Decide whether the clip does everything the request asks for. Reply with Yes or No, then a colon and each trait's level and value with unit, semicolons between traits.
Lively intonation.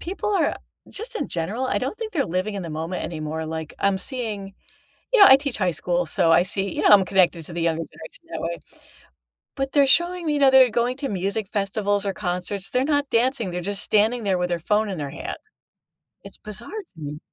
Yes: wide, 7.0 semitones